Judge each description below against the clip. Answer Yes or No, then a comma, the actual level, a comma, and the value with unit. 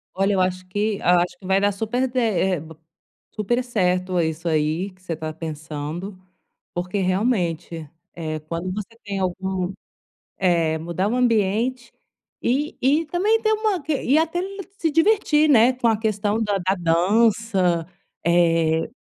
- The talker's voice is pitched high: Yes, high, 195 Hz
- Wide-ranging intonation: Yes, wide, 5.8 semitones